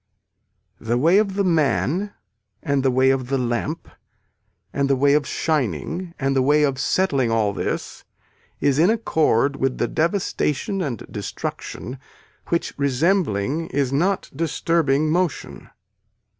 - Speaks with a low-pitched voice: No, medium, 145 Hz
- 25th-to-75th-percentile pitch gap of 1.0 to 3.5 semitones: No, average, 4.2 semitones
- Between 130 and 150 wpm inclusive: Yes, slow, 135 wpm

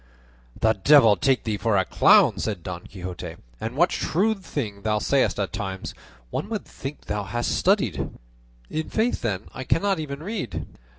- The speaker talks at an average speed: Yes, average, 170 wpm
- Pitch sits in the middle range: No, low, 115 Hz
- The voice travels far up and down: Yes, wide, 7.8 semitones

